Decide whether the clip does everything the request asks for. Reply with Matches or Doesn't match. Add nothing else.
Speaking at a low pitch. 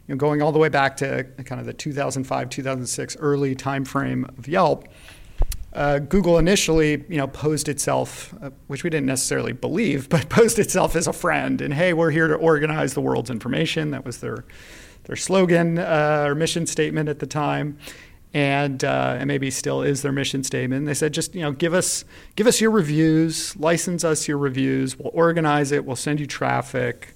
Doesn't match